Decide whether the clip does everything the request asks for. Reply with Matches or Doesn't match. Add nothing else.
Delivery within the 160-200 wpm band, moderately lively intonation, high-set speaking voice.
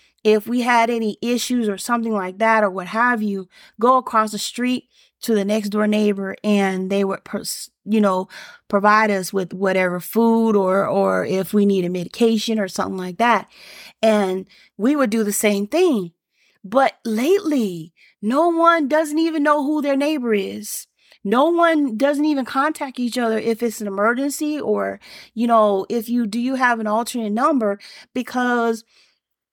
Matches